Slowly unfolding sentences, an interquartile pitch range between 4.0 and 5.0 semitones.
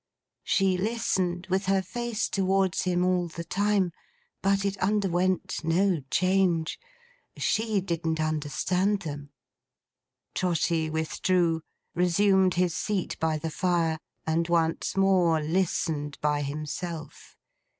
No: slow, 110 wpm; average, 3.0 semitones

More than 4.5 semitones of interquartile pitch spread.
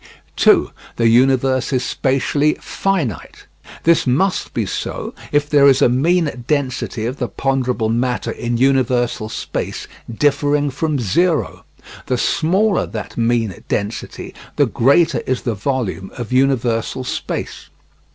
No: average, 3.4 semitones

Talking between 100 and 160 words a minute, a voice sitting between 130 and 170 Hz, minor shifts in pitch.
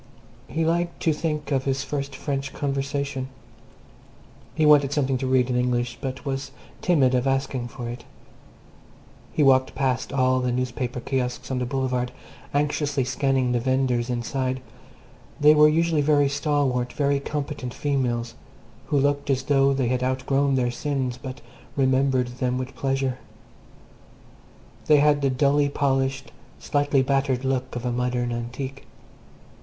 Yes: average, 145 wpm; low, 135 Hz; narrow, 2.0 semitones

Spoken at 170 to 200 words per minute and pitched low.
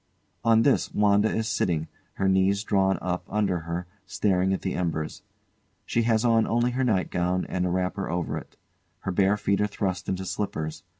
Yes: average, 180 wpm; very low, 95 Hz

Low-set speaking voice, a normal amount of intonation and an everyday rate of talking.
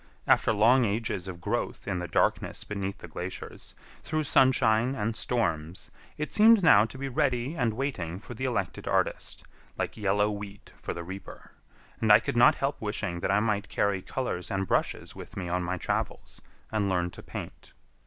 Yes: low, 105 Hz; average, 4.6 semitones; average, 185 wpm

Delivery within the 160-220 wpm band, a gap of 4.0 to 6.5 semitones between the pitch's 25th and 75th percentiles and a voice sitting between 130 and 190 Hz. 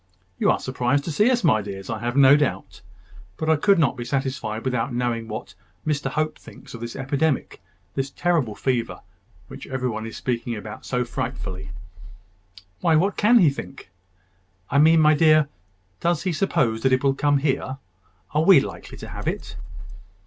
Yes: average, 180 wpm; average, 4.7 semitones; low, 135 Hz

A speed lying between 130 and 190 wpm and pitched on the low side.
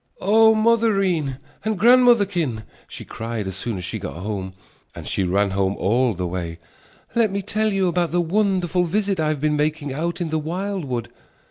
No: average, 185 wpm; medium, 165 Hz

